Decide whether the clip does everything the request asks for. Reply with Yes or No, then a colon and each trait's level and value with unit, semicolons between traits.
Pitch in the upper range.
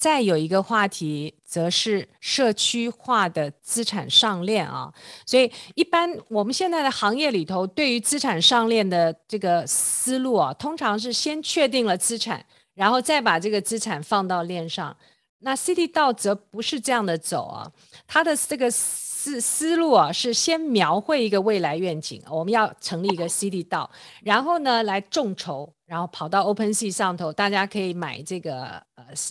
Yes: high, 210 Hz